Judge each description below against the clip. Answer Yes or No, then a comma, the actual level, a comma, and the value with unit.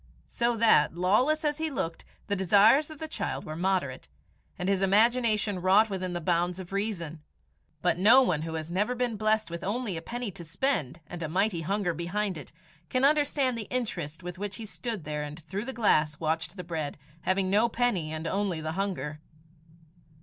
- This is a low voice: No, high, 190 Hz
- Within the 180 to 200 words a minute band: Yes, average, 195 wpm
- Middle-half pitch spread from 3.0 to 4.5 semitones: No, average, 5.2 semitones